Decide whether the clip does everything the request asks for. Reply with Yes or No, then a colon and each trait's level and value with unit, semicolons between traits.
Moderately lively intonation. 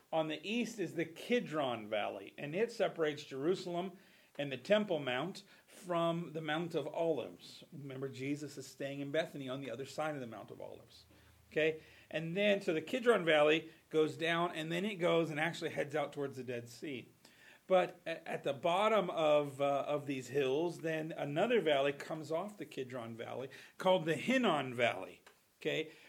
Yes: average, 3.7 semitones